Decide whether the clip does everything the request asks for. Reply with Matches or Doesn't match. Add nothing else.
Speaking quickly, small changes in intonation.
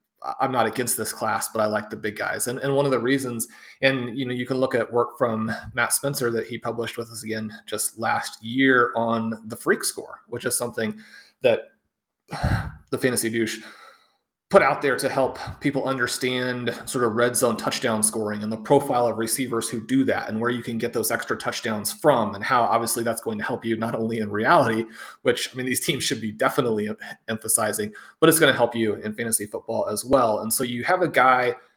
Matches